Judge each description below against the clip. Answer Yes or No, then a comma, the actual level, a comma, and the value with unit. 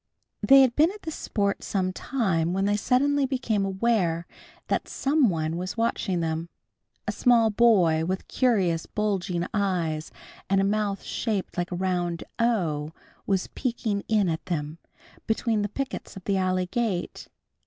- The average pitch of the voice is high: Yes, high, 195 Hz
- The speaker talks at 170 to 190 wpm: No, average, 155 wpm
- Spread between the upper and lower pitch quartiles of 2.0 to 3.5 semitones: No, average, 4.7 semitones